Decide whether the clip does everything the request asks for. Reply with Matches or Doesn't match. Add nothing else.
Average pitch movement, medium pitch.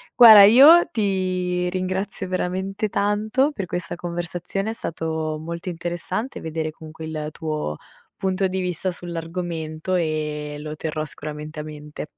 Matches